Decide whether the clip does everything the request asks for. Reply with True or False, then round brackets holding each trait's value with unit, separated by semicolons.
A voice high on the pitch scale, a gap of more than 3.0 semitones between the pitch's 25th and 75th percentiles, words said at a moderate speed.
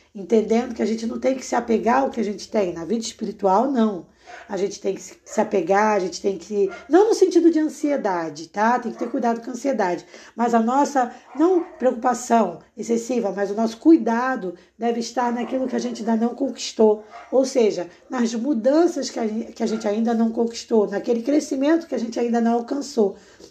False (235 Hz; 3.7 semitones; 200 wpm)